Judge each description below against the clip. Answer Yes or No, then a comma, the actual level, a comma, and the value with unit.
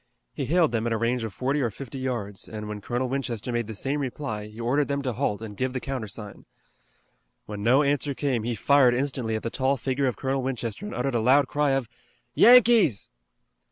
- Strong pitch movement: No, average, 3.5 semitones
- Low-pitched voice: Yes, low, 125 Hz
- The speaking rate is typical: No, fast, 215 wpm